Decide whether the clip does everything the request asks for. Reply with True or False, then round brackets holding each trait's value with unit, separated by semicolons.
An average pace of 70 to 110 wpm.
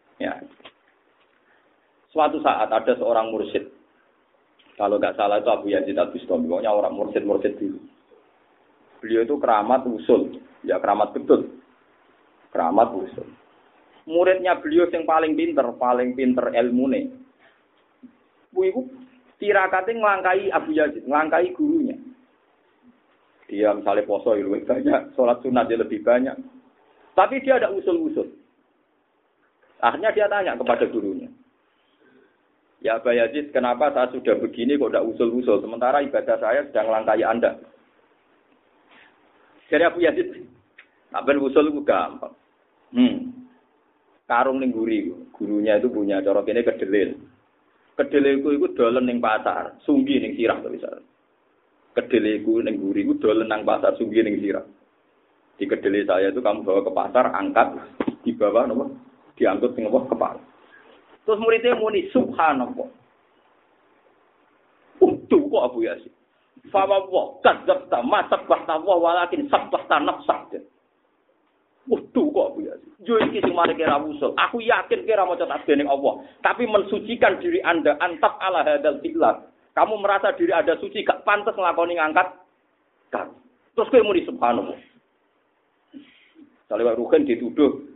False (125 wpm)